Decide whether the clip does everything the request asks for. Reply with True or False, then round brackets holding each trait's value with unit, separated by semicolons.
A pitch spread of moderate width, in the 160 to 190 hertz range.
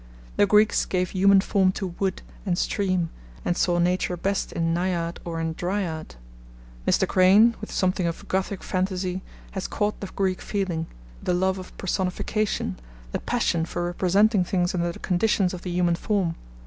False (2.0 semitones; 185 Hz)